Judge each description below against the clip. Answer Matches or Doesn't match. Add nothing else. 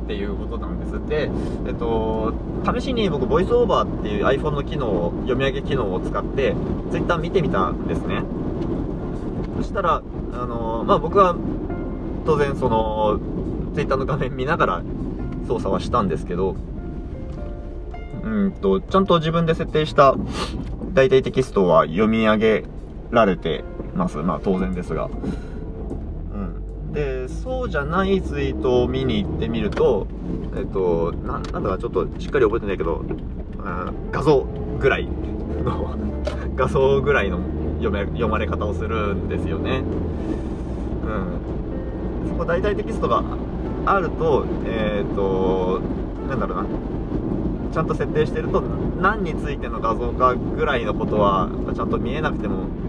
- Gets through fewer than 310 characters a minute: Matches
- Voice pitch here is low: Matches